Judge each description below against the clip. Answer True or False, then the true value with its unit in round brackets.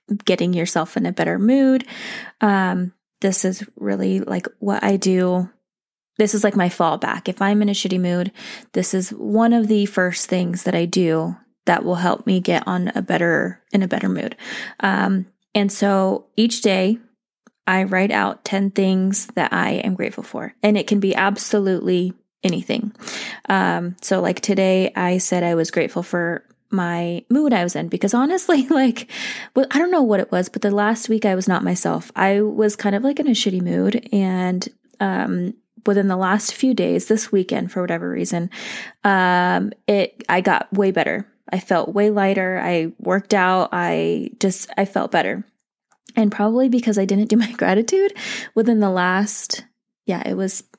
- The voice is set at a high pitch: True (200 Hz)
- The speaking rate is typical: True (180 wpm)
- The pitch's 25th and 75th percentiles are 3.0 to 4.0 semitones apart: True (3.3 semitones)